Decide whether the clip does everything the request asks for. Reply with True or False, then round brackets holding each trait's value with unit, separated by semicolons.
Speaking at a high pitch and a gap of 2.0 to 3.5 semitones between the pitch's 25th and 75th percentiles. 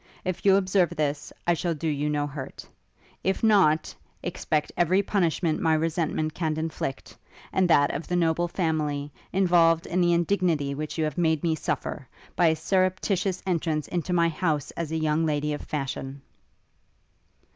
False (160 Hz; 2.7 semitones)